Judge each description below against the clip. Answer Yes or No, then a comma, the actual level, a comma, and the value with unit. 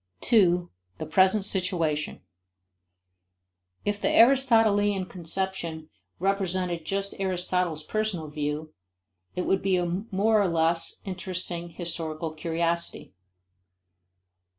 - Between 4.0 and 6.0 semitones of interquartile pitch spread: No, average, 2.9 semitones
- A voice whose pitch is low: No, medium, 180 Hz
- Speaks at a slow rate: Yes, slow, 95 wpm